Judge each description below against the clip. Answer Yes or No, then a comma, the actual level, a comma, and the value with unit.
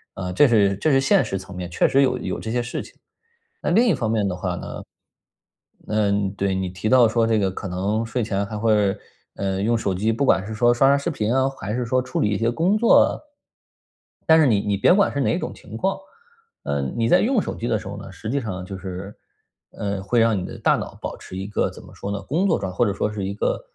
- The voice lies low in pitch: Yes, low, 110 Hz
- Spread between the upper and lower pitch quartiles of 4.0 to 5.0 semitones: Yes, average, 4.3 semitones